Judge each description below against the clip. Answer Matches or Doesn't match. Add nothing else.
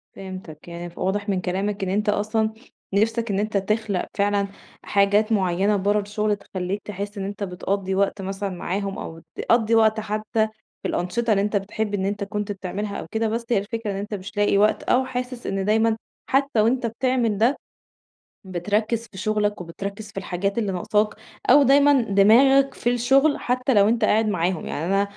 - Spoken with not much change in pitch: Matches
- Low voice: Doesn't match